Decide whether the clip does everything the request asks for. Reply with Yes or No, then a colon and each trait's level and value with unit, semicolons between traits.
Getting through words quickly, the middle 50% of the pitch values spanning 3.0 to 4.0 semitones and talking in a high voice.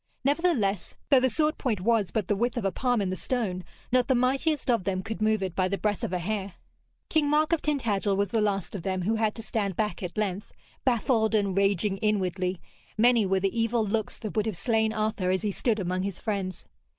Yes: fast, 230 wpm; average, 3.5 semitones; high, 215 Hz